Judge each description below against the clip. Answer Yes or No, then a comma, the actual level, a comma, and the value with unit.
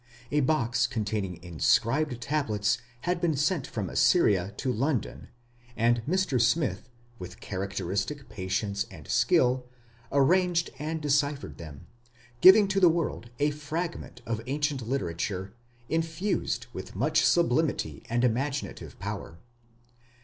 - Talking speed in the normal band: No, slow, 120 wpm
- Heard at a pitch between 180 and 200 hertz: No, low, 130 Hz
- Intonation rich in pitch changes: Yes, wide, 6.8 semitones